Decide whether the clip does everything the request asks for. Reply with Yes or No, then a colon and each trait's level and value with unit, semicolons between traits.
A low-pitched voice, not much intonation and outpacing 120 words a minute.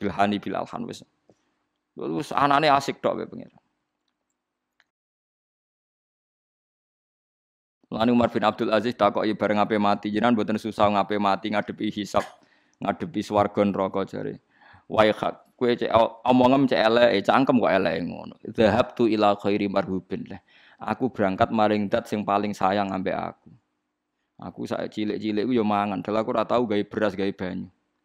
Yes: low, 105 Hz; narrow, 1.5 semitones; fast, 140 wpm